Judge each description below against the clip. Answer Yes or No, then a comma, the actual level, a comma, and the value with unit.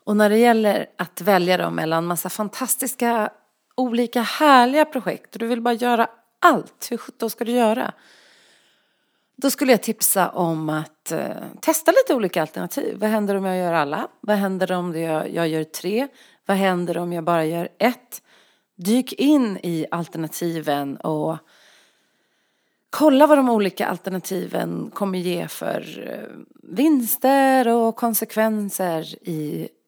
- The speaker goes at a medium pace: Yes, average, 150 wpm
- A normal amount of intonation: No, wide, 5.7 semitones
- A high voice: Yes, high, 210 Hz